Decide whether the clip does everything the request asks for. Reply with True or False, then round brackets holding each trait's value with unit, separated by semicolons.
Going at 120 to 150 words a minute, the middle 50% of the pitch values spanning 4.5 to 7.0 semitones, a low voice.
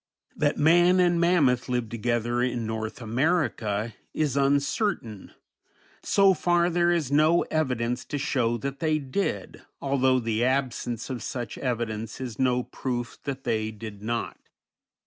True (140 wpm; 4.8 semitones; 130 Hz)